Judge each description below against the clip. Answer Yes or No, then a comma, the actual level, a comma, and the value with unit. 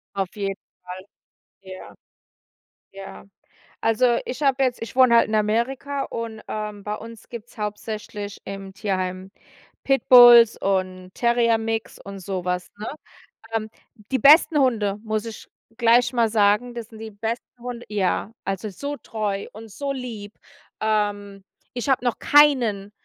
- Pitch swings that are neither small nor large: Yes, average, 3.1 semitones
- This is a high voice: Yes, high, 220 Hz